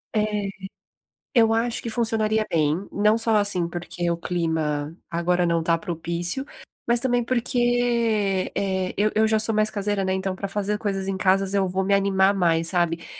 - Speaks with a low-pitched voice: No, high, 195 Hz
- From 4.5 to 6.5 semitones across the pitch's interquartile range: No, average, 3.8 semitones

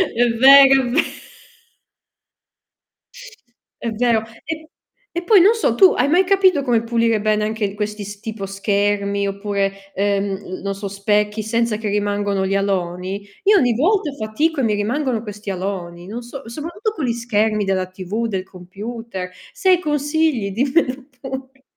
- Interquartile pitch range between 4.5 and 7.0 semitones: Yes, average, 5.1 semitones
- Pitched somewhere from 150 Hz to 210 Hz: No, high, 220 Hz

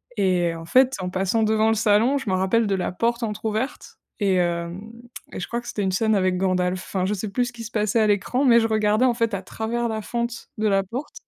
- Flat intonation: No, average, 3.6 semitones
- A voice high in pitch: Yes, high, 215 Hz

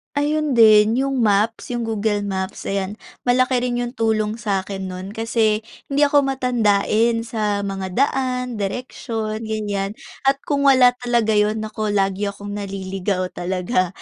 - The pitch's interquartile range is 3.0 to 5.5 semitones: Yes, average, 3.5 semitones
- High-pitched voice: Yes, high, 215 Hz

